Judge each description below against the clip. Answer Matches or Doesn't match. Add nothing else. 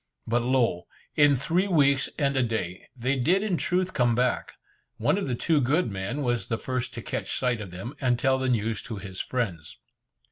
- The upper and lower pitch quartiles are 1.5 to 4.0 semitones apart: Matches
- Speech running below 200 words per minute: Doesn't match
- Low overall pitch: Matches